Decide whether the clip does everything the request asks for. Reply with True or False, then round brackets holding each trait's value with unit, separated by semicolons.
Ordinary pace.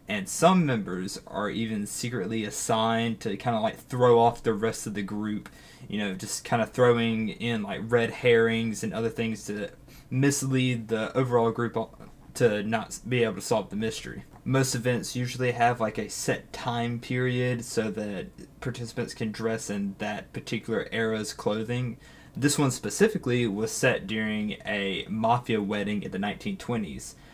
True (165 wpm)